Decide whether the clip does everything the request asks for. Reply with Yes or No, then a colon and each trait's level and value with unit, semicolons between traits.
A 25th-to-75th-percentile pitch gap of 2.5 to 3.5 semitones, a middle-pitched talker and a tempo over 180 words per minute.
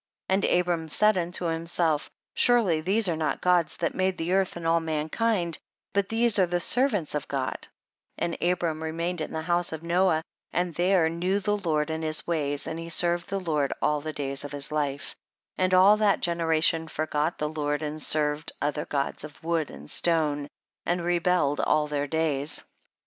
Yes: average, 2.8 semitones; medium, 165 Hz; average, 190 wpm